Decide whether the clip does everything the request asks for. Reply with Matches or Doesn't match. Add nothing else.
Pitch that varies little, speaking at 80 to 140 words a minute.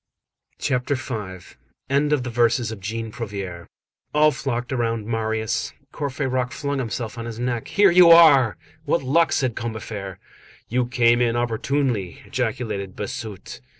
Doesn't match